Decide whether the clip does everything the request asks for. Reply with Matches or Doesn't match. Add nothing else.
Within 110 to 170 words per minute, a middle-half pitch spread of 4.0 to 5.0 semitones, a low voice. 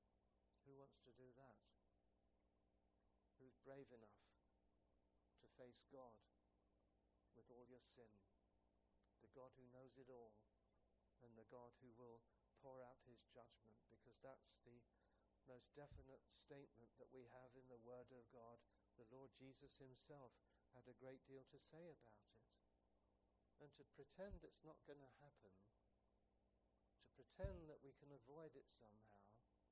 Matches